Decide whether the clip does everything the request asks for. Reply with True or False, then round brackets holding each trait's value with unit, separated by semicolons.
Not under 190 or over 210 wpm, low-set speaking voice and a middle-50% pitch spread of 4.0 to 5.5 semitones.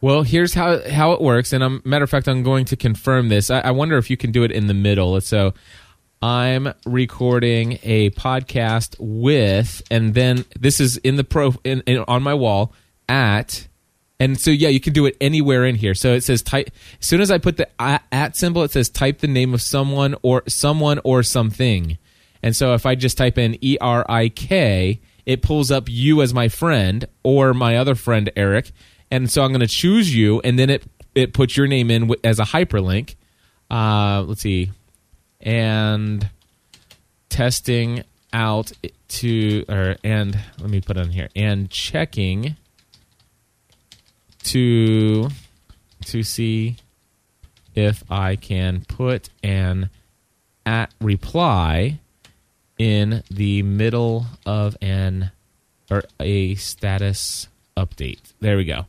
False (160 wpm; 115 Hz; 4.3 semitones)